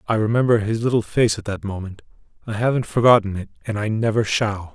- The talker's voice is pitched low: Yes, low, 105 Hz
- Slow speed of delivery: No, average, 200 wpm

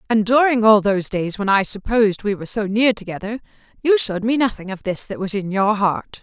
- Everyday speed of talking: No, fast, 220 wpm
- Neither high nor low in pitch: No, high, 215 Hz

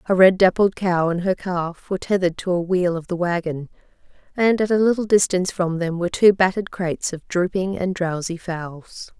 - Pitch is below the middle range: No, medium, 180 Hz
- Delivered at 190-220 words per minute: Yes, average, 200 wpm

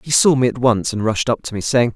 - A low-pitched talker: Yes, low, 120 Hz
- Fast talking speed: Yes, fast, 340 wpm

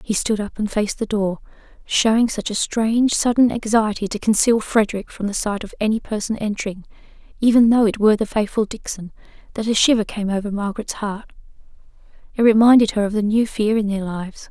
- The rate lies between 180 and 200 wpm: Yes, average, 195 wpm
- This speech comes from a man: No, female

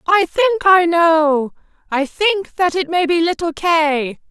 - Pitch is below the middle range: No, very high, 335 Hz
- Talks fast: No, average, 165 wpm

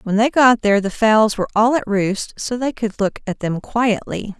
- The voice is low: No, high, 220 Hz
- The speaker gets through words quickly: Yes, fast, 230 wpm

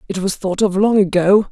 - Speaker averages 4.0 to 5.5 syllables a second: Yes, 5.4 syllables/s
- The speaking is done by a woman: Yes, female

